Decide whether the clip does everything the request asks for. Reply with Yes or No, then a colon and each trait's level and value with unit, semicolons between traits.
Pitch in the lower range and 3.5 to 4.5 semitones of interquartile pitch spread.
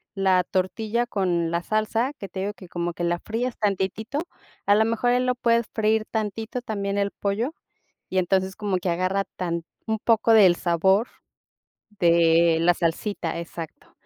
No: high, 200 Hz; average, 4.0 semitones